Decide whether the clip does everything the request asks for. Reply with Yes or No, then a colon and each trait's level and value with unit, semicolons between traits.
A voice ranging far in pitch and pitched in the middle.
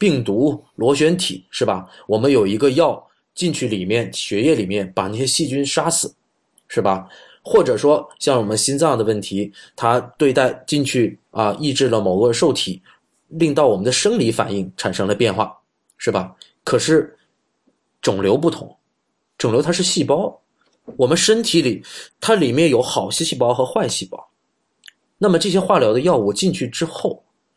Yes: wide, 6.7 semitones; medium, 145 Hz